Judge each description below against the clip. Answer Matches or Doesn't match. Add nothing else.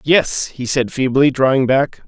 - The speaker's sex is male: Matches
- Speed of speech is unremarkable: Matches